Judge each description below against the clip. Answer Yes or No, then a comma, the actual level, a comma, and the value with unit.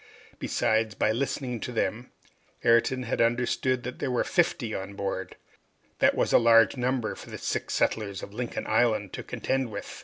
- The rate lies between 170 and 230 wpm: Yes, average, 175 wpm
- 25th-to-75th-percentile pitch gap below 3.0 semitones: Yes, narrow, 2.5 semitones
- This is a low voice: Yes, low, 115 Hz